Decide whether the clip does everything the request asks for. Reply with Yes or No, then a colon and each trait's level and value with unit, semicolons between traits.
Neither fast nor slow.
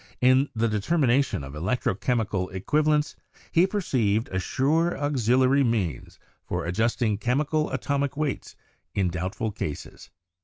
No: slow, 125 wpm